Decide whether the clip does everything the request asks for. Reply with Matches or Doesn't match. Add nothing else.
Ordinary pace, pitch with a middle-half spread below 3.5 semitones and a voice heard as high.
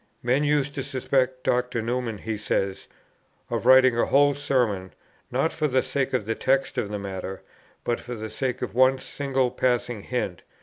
Doesn't match